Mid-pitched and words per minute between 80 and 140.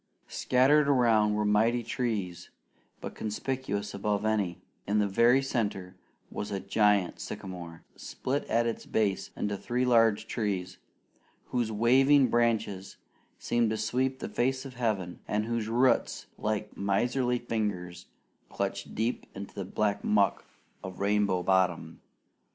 No: low, 105 Hz; slow, 135 wpm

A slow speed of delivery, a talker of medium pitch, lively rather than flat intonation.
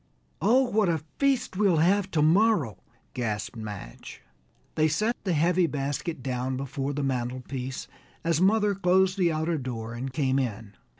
No: average, 155 wpm; medium, 155 Hz; wide, 6.5 semitones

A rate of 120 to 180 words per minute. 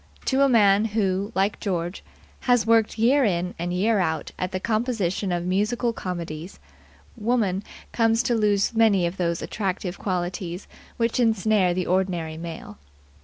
Yes: average, 150 wpm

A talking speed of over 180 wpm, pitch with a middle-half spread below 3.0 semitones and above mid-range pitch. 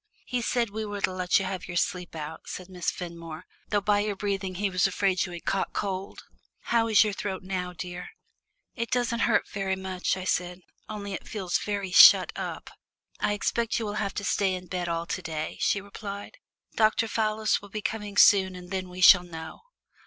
Yes: fast, 205 wpm; narrow, 2.5 semitones; high, 195 Hz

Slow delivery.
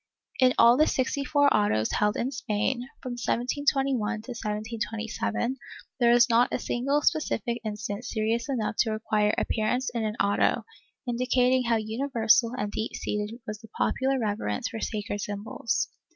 No: average, 150 wpm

